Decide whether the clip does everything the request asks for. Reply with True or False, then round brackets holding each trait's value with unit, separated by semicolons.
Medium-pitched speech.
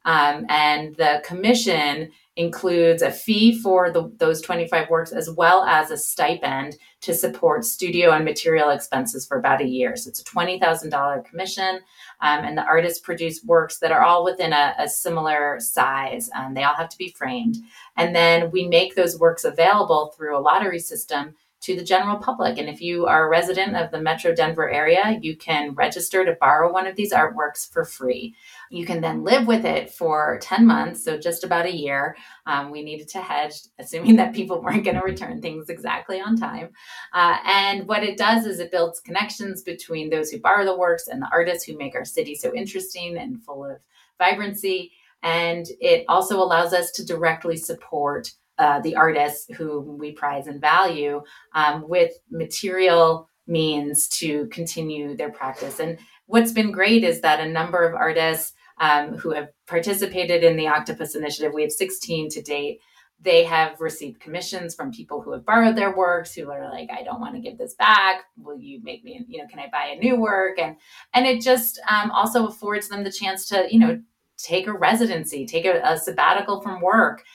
True (175 Hz)